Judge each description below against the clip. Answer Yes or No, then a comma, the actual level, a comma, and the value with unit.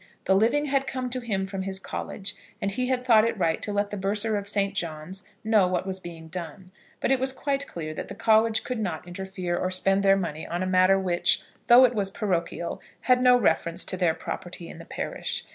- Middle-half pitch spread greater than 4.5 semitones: No, average, 3.8 semitones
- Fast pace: Yes, fast, 230 wpm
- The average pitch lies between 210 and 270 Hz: No, high, 195 Hz